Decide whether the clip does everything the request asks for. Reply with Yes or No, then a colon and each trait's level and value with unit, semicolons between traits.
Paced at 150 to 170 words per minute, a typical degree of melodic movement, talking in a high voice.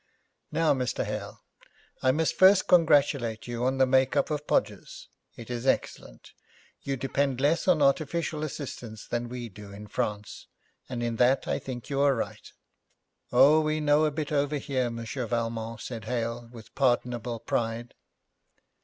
No: average, 160 wpm; average, 3.7 semitones; low, 125 Hz